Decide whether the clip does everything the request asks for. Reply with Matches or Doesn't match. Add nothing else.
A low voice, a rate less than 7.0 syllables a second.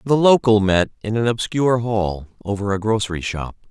Matches